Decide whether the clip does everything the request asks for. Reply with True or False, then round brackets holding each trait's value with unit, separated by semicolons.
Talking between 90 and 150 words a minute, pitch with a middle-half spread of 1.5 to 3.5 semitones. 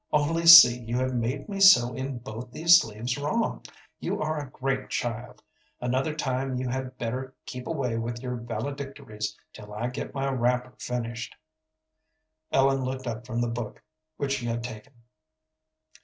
False (160 wpm; 2.4 semitones)